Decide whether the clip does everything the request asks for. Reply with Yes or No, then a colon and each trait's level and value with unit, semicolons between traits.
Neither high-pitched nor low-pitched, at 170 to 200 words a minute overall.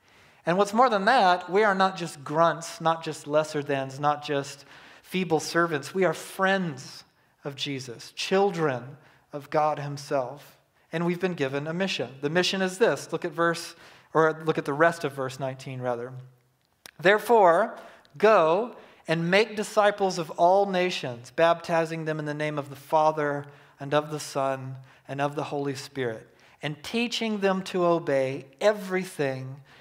No: medium, 155 Hz; average, 160 wpm